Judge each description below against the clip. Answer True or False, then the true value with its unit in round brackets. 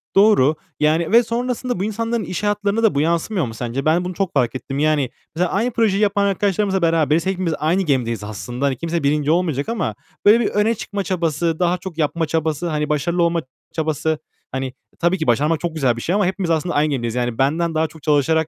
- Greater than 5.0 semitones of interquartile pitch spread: False (4.7 semitones)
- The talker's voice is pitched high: False (165 Hz)